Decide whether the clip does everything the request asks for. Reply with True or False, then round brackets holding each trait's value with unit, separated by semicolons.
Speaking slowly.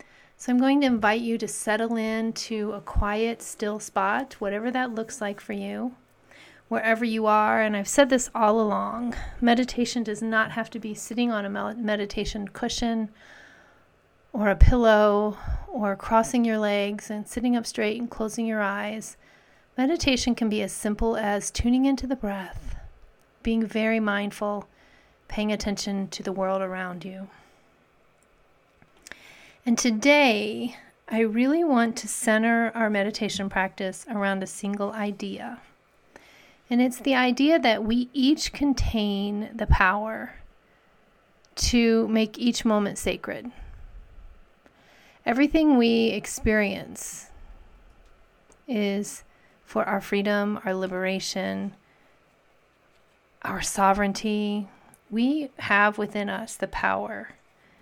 True (125 wpm)